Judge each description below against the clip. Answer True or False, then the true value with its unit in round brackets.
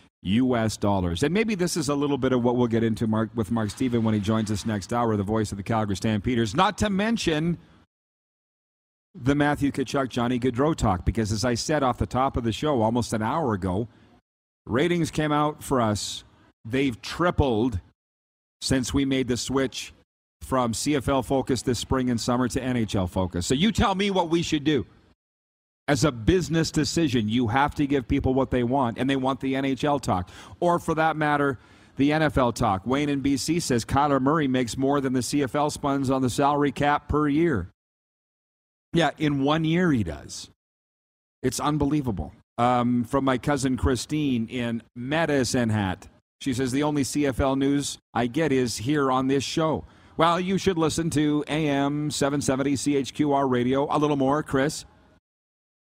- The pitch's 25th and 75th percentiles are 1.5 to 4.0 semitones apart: False (4.6 semitones)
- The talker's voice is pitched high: False (130 Hz)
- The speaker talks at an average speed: True (180 wpm)